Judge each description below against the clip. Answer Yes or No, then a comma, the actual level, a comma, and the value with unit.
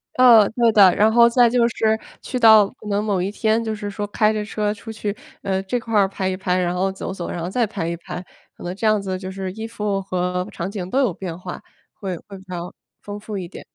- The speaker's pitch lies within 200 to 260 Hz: Yes, high, 205 Hz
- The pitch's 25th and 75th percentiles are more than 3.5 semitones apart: No, average, 2.7 semitones